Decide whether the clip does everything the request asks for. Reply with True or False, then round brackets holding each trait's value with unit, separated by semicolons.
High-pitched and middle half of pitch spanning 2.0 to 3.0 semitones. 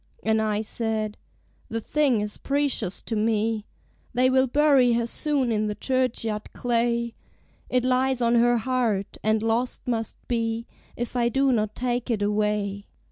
True (235 Hz; 2.7 semitones)